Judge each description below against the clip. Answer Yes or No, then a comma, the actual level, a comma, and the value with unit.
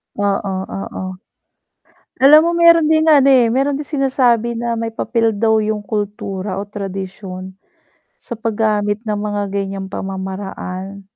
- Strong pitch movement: No, average, 3.3 semitones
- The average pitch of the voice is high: Yes, high, 210 Hz